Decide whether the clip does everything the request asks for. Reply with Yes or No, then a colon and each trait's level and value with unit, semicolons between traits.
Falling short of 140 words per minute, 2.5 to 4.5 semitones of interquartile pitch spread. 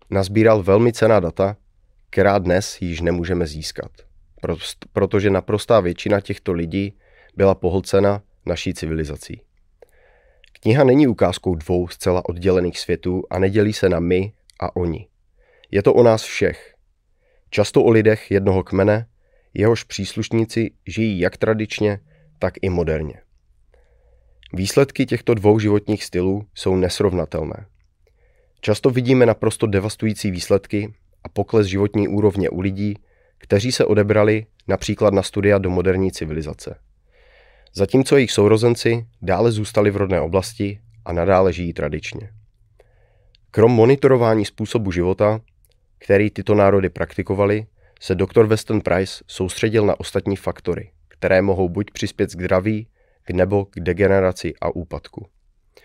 Yes: average, 125 wpm; average, 2.8 semitones